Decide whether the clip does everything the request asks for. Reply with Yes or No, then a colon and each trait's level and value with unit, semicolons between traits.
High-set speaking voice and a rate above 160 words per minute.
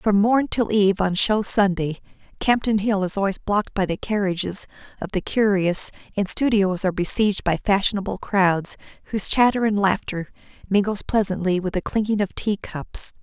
Yes: high, 200 Hz; average, 170 wpm